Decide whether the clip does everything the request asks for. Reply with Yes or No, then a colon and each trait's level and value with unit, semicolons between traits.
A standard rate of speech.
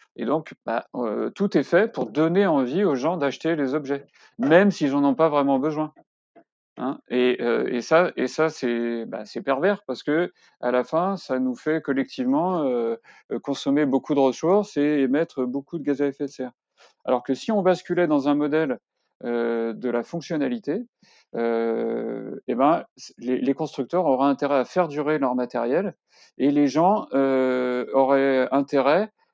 Yes: average, 180 wpm